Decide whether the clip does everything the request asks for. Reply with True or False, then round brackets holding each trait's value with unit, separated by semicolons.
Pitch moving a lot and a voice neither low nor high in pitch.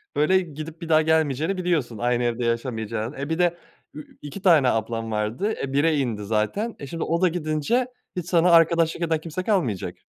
True (5.9 semitones; 155 Hz)